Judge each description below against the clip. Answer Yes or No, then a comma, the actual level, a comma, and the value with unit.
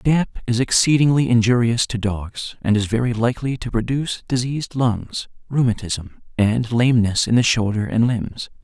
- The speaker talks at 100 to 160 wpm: Yes, average, 155 wpm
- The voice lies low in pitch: Yes, low, 120 Hz